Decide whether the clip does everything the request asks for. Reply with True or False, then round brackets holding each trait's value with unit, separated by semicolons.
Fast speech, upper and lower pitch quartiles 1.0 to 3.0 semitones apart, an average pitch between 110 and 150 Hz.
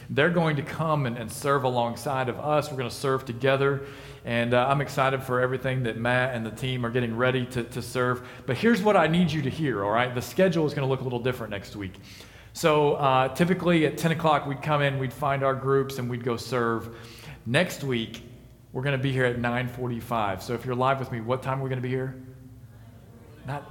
True (240 wpm; 2.6 semitones; 130 Hz)